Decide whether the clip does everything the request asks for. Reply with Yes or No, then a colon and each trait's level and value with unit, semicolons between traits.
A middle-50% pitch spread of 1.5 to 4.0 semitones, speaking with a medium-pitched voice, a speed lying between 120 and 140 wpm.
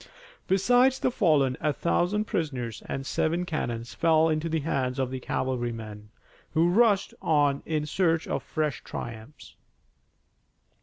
No: average, 5.0 semitones; medium, 155 Hz; slow, 135 wpm